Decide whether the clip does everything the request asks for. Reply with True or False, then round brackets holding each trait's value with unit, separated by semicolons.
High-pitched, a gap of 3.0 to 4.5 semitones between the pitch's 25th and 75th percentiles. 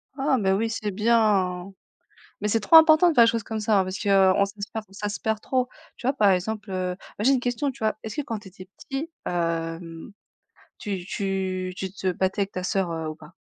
True (200 Hz; 3.4 semitones)